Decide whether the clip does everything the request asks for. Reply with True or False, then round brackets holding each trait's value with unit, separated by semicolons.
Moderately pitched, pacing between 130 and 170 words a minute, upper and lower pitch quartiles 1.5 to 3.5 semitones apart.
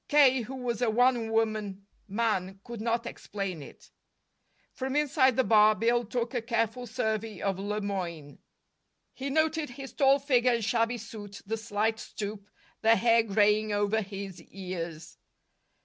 False (225 Hz; 150 wpm; 3.2 semitones)